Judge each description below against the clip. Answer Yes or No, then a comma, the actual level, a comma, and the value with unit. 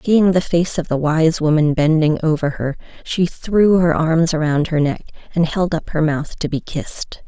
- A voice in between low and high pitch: Yes, medium, 160 Hz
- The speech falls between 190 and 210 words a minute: Yes, fast, 205 wpm